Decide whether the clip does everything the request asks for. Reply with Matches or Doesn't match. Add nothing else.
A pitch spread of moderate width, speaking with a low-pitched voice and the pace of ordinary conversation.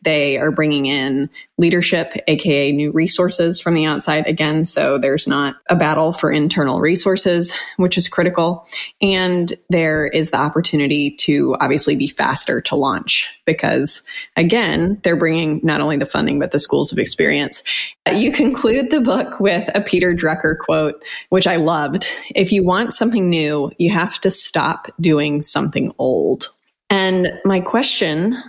Doesn't match